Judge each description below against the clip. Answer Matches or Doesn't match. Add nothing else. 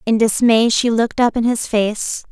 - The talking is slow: Doesn't match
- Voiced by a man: Doesn't match